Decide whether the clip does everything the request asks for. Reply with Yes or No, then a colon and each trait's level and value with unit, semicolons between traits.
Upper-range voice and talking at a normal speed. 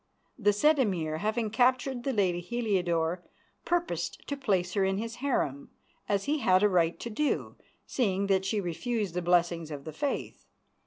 Yes: high, 200 Hz; average, 170 wpm